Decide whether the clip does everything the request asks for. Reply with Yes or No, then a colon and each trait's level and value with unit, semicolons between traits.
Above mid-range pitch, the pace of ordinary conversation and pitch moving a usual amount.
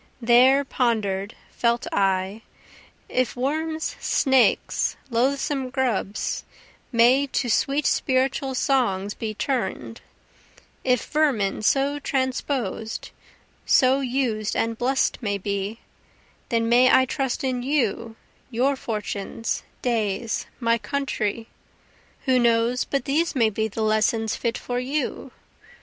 No: high, 245 Hz; slow, 110 wpm; average, 3.4 semitones